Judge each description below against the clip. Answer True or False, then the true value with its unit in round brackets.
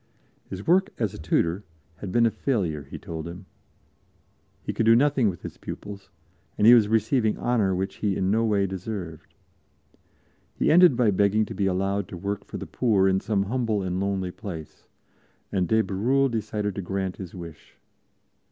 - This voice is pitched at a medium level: False (100 Hz)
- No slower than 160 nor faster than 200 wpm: True (180 wpm)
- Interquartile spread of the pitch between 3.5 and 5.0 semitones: False (3.1 semitones)